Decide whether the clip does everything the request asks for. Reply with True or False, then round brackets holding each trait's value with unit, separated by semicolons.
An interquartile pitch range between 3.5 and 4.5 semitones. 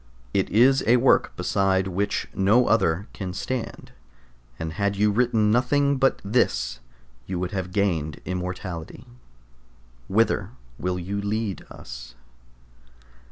True (3.8 semitones)